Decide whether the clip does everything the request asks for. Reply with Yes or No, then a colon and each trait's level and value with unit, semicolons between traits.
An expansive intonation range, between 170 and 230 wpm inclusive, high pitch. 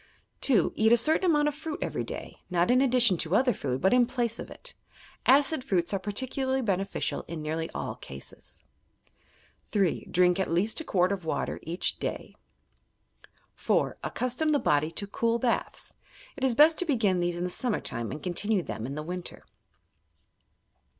Yes: wide, 6.9 semitones; average, 175 wpm; high, 205 Hz